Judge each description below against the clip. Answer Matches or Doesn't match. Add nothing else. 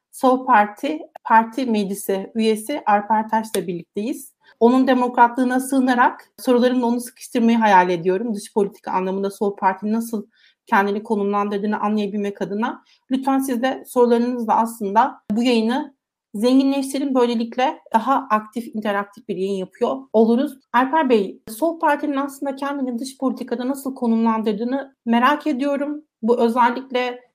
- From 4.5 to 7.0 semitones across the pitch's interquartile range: Doesn't match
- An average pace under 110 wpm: Doesn't match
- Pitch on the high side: Matches